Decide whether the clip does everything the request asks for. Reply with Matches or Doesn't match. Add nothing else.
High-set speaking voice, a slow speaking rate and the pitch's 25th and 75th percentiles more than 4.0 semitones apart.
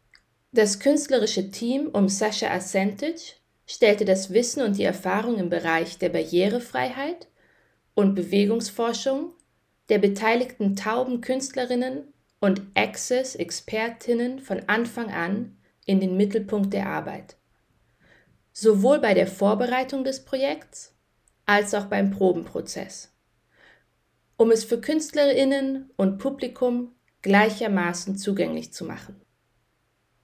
Matches